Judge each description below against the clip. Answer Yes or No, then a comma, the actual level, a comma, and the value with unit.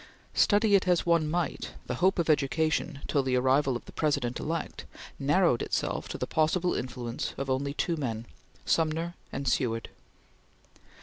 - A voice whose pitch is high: No, medium, 150 Hz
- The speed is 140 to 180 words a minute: Yes, average, 160 wpm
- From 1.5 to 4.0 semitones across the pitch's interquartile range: No, average, 4.4 semitones